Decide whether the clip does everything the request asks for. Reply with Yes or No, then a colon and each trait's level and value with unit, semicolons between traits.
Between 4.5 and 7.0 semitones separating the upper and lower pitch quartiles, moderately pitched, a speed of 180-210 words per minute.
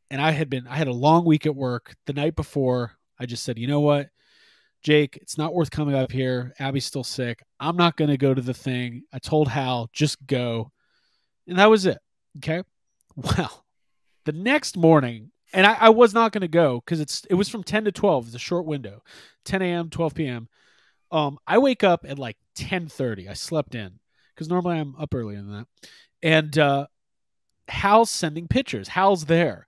Yes: average, 5.1 semitones; medium, 150 Hz; average, 200 wpm